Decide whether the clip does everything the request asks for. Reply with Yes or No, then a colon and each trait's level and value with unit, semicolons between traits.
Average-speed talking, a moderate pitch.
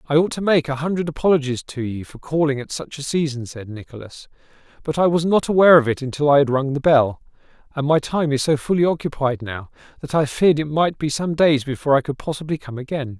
No: fast, 235 wpm; medium, 145 Hz